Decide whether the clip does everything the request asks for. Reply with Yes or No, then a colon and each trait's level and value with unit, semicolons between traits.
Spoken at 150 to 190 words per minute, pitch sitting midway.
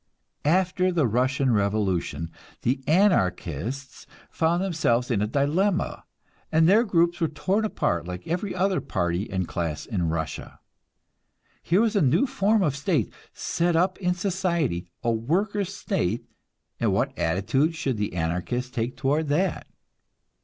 No: average, 140 wpm; medium, 145 Hz